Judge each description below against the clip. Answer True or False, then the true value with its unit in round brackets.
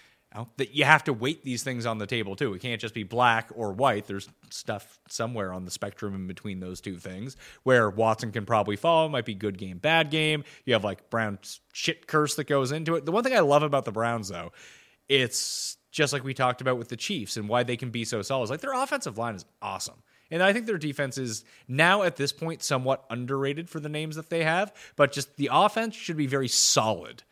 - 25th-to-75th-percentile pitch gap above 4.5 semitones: True (5.3 semitones)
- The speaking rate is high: True (235 wpm)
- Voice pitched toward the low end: True (130 Hz)